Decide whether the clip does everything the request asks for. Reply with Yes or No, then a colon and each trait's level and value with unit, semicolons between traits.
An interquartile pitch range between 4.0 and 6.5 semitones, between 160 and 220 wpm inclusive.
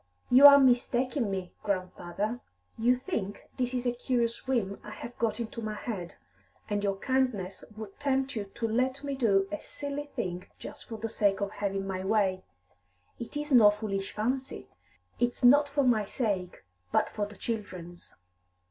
Yes: average, 4.3 semitones; average, 165 wpm